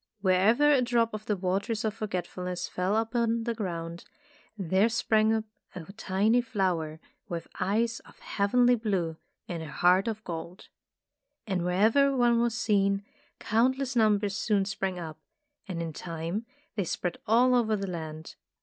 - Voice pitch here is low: No, high, 205 Hz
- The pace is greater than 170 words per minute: No, average, 150 wpm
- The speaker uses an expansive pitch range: No, average, 4.0 semitones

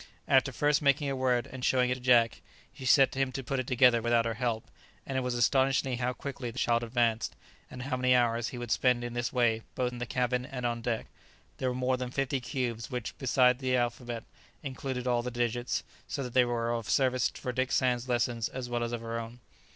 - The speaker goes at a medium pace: No, fast, 230 wpm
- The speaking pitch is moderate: No, low, 125 Hz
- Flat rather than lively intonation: Yes, narrow, 1.4 semitones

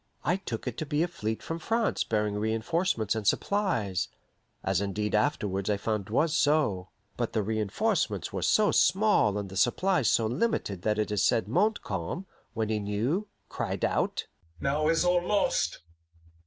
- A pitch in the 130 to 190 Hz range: No, low, 115 Hz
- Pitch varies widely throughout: Yes, wide, 8.3 semitones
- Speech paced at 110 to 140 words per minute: No, average, 170 wpm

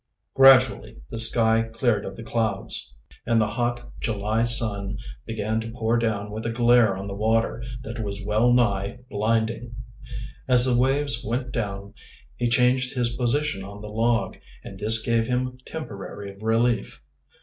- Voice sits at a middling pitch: No, low, 115 Hz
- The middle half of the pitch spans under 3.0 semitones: Yes, narrow, 2.4 semitones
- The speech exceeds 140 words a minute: Yes, average, 155 wpm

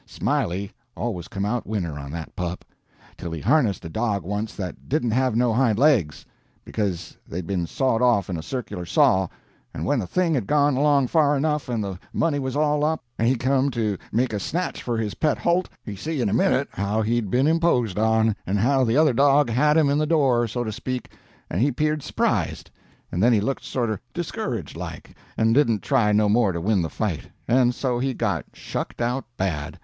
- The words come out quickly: Yes, fast, 210 wpm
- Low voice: Yes, low, 120 Hz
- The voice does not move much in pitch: No, wide, 5.5 semitones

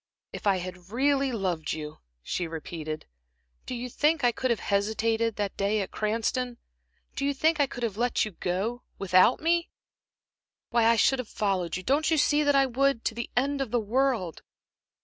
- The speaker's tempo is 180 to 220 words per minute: Yes, average, 190 wpm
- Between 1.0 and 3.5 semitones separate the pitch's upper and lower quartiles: No, wide, 5.5 semitones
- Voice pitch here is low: No, high, 230 Hz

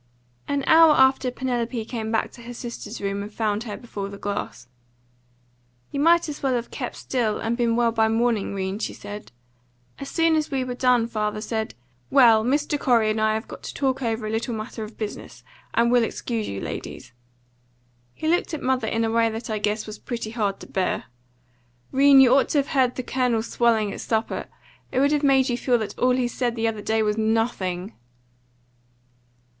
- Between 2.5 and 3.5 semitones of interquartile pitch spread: Yes, average, 3.0 semitones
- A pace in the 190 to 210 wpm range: Yes, fast, 205 wpm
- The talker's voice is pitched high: Yes, high, 230 Hz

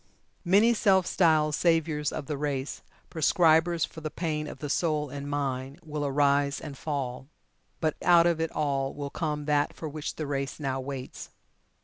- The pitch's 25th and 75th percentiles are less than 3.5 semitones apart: Yes, narrow, 2.4 semitones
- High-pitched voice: No, medium, 150 Hz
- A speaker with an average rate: Yes, average, 170 wpm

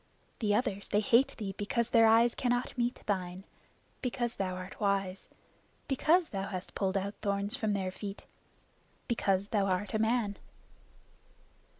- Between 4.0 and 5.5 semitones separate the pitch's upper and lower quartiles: No, average, 3.4 semitones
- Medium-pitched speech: No, high, 205 Hz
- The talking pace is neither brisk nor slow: Yes, average, 150 wpm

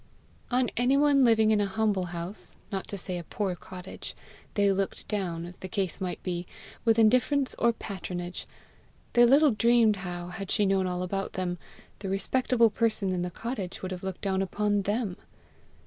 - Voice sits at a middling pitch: No, high, 195 Hz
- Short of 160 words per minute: No, average, 180 wpm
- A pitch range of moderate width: Yes, average, 3.8 semitones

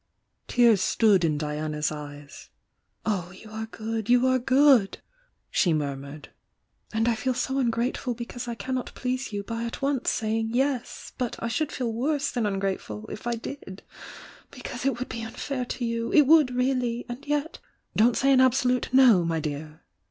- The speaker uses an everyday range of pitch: Yes, average, 4.5 semitones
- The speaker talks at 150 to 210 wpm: Yes, average, 180 wpm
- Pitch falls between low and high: No, high, 235 Hz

